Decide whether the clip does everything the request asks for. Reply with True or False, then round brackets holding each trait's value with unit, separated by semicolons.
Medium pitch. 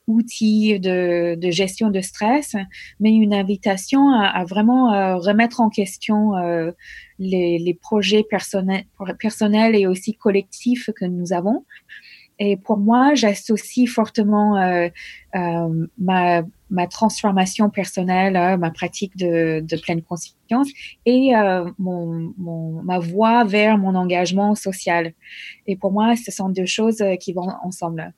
False (195 Hz)